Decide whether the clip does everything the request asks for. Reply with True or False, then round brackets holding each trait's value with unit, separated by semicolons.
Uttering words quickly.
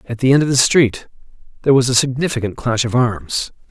True (210 wpm)